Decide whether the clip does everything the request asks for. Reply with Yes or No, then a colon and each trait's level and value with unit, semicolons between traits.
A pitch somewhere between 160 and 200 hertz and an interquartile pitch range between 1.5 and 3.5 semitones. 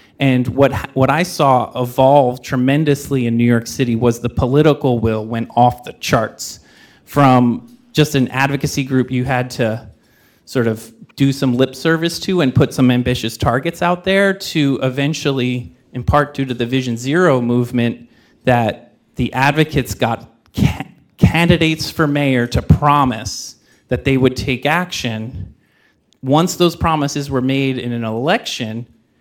No: low, 130 Hz; average, 3.1 semitones